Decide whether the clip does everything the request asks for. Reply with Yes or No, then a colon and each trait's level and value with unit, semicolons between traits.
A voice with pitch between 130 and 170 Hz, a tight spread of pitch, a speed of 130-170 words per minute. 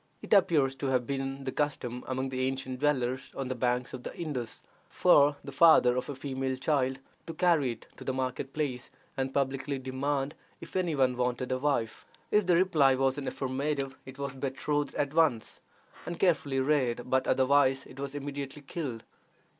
No: low, 135 Hz; narrow, 2.1 semitones; average, 185 wpm